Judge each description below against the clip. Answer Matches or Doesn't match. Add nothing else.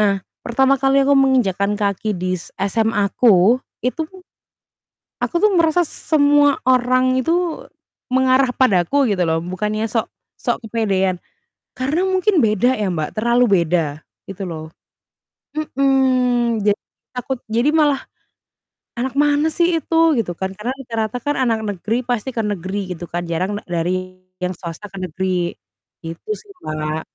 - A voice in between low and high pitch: Doesn't match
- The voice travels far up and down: Matches